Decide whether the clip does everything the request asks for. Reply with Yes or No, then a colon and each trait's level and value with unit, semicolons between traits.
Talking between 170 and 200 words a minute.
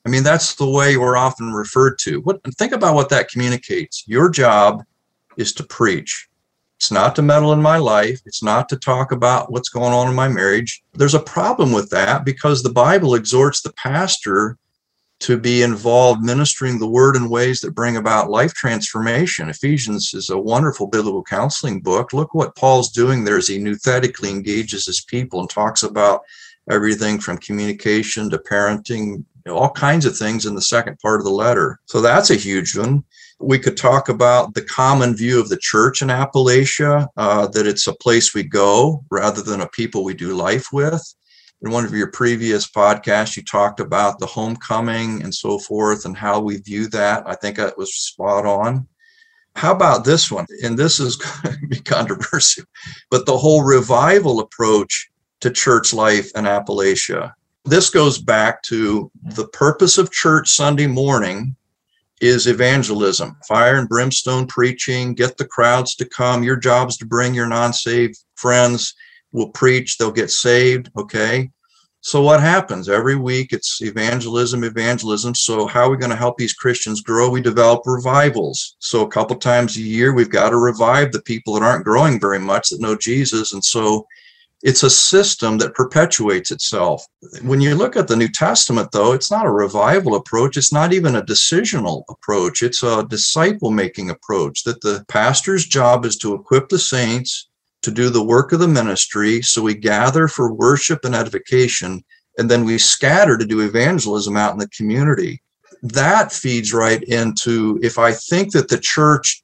Yes: average, 180 wpm